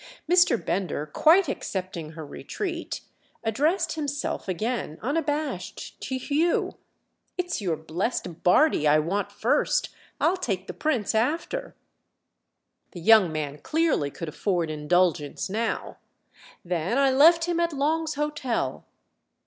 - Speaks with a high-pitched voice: Yes, high, 230 Hz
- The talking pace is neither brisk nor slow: No, slow, 115 wpm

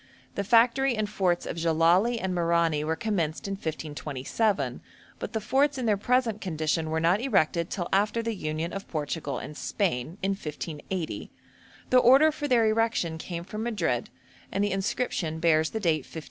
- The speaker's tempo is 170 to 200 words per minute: Yes, average, 175 wpm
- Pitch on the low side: No, medium, 185 Hz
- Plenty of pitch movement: Yes, wide, 5.7 semitones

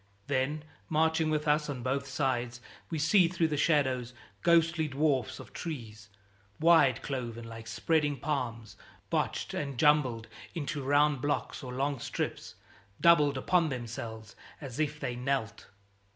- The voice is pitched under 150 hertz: Yes, medium, 140 Hz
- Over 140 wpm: No, slow, 135 wpm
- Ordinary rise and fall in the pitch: Yes, average, 3.8 semitones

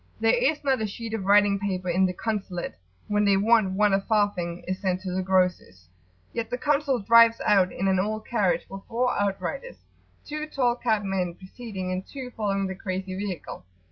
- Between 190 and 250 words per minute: Yes, average, 195 wpm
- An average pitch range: Yes, average, 3.5 semitones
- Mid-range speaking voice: No, high, 200 Hz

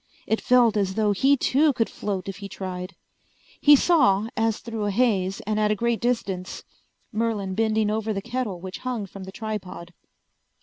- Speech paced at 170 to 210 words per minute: Yes, average, 180 wpm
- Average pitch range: Yes, average, 3.1 semitones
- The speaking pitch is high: Yes, high, 215 Hz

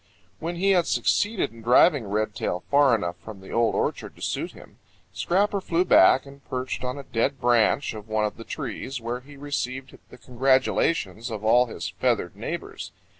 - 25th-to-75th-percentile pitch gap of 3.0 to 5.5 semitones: Yes, average, 4.3 semitones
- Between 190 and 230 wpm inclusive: No, average, 180 wpm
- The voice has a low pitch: Yes, low, 125 Hz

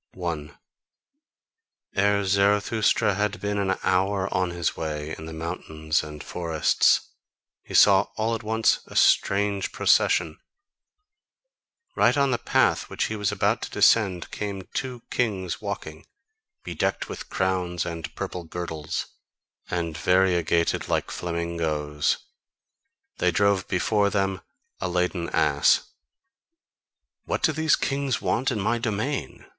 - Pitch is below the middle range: Yes, very low, 95 Hz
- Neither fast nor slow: No, slow, 125 wpm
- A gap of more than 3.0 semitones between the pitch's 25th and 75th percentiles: Yes, average, 3.6 semitones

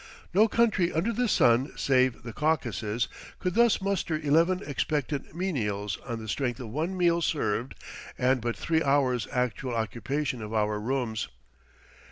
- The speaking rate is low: No, average, 150 wpm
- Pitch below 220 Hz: Yes, low, 135 Hz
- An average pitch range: No, wide, 6.3 semitones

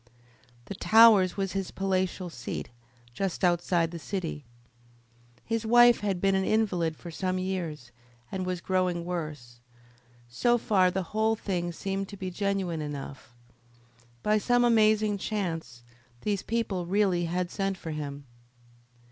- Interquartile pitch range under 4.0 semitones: Yes, average, 3.1 semitones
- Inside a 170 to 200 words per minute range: No, average, 140 wpm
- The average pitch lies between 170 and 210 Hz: Yes, medium, 185 Hz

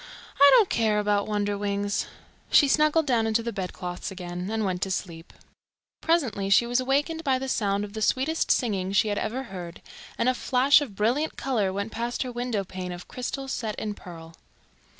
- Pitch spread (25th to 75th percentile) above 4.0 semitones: Yes, average, 4.7 semitones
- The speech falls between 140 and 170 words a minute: No, average, 190 wpm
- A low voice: No, high, 215 Hz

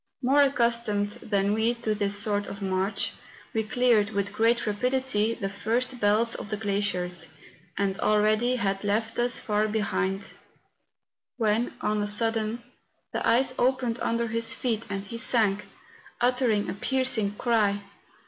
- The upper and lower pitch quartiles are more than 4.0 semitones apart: No, narrow, 2.6 semitones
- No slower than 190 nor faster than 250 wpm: No, average, 145 wpm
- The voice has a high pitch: Yes, high, 215 Hz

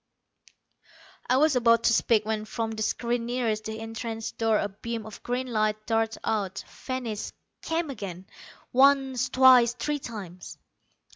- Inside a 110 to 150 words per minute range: Yes, average, 145 wpm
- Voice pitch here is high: Yes, high, 230 Hz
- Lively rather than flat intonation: No, narrow, 2.6 semitones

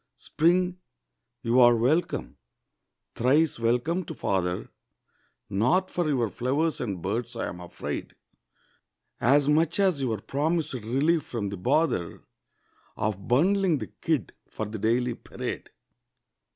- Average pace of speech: No, slow, 120 wpm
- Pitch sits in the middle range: No, low, 130 Hz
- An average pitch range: No, wide, 6.3 semitones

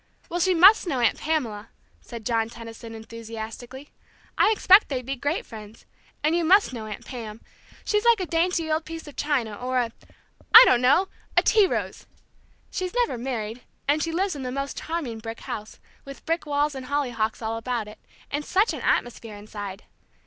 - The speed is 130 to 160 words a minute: No, average, 185 wpm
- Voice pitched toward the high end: Yes, very high, 260 Hz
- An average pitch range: No, wide, 6.4 semitones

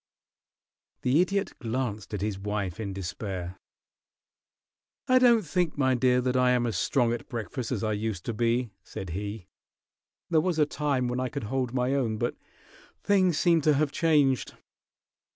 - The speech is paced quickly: No, average, 170 wpm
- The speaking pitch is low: Yes, low, 125 Hz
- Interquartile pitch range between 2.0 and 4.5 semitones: No, wide, 5.6 semitones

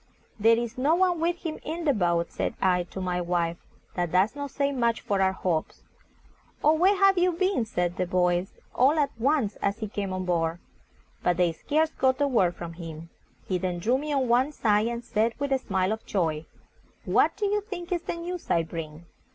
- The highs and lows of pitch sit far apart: Yes, wide, 8.9 semitones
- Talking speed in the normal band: No, fast, 215 wpm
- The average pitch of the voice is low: No, high, 220 Hz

